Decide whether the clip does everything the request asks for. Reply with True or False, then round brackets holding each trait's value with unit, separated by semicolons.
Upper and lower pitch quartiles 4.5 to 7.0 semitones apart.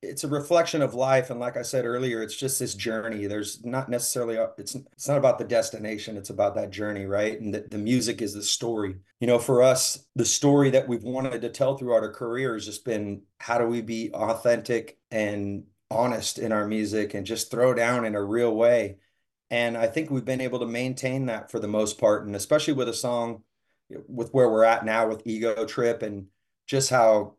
False (2.9 semitones)